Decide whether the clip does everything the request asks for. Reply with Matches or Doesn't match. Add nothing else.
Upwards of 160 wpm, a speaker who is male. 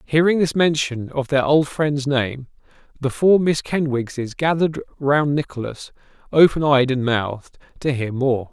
Doesn't match